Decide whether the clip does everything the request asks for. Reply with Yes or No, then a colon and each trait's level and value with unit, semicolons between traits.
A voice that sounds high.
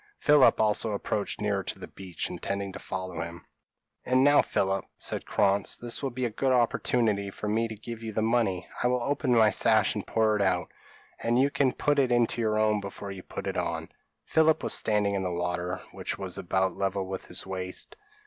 No: low, 105 Hz